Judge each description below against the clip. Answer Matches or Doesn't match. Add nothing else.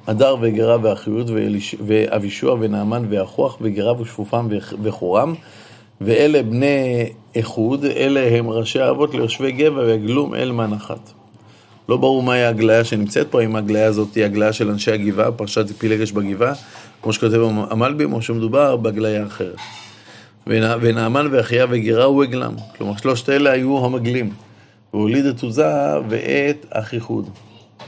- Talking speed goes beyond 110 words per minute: Matches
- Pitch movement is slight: Matches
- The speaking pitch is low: Matches